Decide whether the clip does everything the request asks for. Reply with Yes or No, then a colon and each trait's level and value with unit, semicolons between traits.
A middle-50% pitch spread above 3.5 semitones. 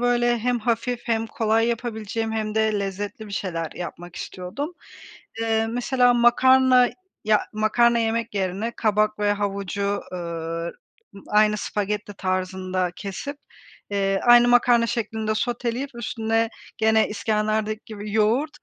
No: average, 2.7 semitones